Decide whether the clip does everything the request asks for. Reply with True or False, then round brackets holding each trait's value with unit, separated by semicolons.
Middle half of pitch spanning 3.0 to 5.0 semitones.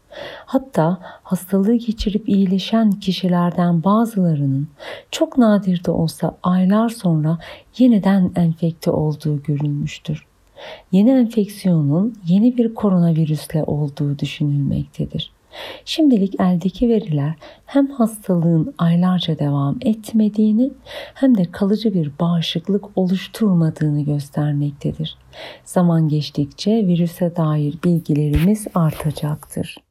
False (5.4 semitones)